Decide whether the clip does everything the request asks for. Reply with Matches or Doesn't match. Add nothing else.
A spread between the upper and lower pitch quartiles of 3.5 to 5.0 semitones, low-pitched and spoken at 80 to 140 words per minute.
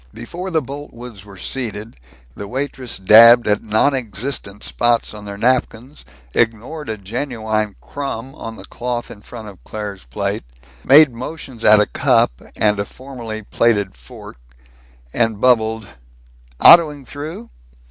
Matches